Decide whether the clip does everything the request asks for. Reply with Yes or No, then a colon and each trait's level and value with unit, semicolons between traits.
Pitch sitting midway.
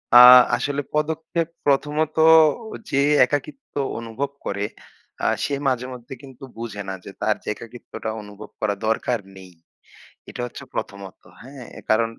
No: low, 125 Hz